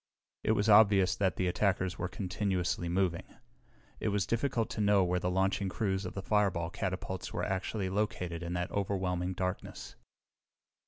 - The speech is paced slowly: No, average, 160 wpm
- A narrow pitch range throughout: Yes, narrow, 2.1 semitones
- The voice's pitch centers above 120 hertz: No, very low, 95 Hz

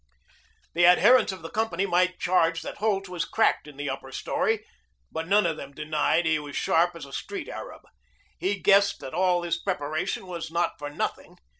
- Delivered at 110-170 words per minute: No, average, 190 wpm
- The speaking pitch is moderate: Yes, medium, 175 Hz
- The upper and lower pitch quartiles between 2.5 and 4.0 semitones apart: Yes, average, 3.4 semitones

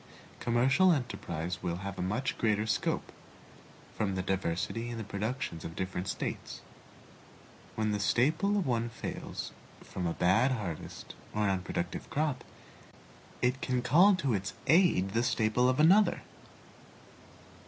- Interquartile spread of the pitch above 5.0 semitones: Yes, wide, 5.5 semitones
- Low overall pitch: Yes, low, 115 Hz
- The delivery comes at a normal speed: No, slow, 130 wpm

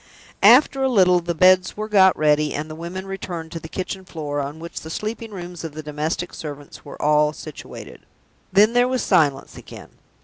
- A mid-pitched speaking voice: Yes, medium, 170 Hz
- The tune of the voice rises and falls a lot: No, average, 4.0 semitones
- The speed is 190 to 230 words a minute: Yes, average, 195 wpm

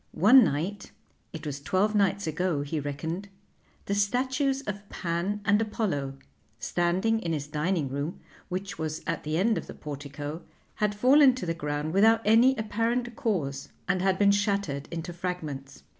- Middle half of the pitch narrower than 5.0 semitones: No, wide, 5.6 semitones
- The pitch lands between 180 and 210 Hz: Yes, medium, 185 Hz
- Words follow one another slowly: No, average, 160 wpm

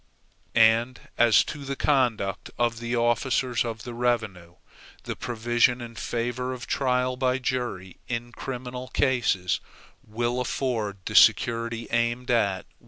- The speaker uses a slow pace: Yes, slow, 130 wpm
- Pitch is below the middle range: Yes, low, 120 Hz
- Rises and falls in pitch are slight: Yes, narrow, 1.7 semitones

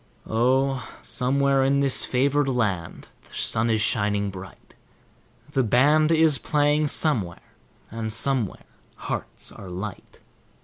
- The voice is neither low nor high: No, low, 125 Hz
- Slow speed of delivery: Yes, slow, 120 wpm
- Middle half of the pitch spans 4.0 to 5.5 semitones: Yes, average, 4.6 semitones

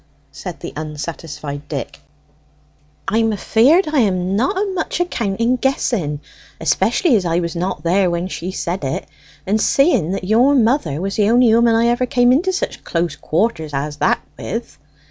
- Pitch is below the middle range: No, high, 200 Hz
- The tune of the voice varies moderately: No, wide, 6.5 semitones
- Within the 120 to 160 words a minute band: No, average, 170 wpm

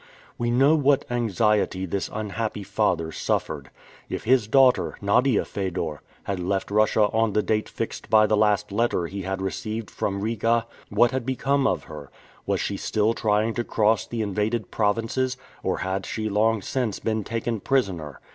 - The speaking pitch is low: Yes, low, 110 Hz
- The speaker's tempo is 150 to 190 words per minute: Yes, average, 165 wpm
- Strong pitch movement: No, average, 2.9 semitones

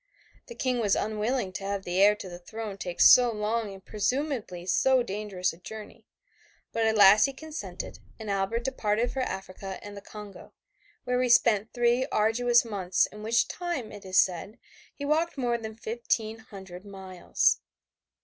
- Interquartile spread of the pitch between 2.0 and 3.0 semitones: No, average, 3.7 semitones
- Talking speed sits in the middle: Yes, average, 170 wpm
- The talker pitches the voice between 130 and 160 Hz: No, high, 215 Hz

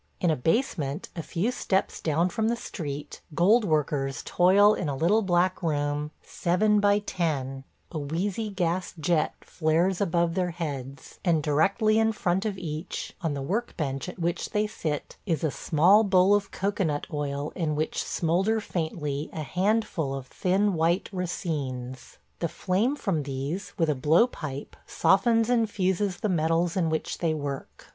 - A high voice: No, medium, 170 Hz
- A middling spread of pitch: Yes, average, 4.7 semitones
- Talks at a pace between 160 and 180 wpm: Yes, average, 165 wpm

